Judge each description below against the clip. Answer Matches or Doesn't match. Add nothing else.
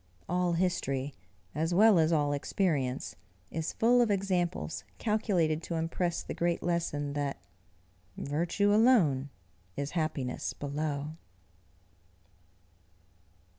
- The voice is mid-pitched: Matches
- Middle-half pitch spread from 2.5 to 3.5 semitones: Doesn't match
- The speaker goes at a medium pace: Doesn't match